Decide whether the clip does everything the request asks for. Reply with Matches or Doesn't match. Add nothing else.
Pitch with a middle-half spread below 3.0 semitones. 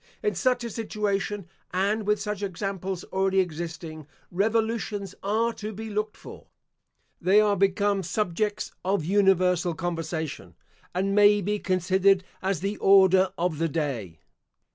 Matches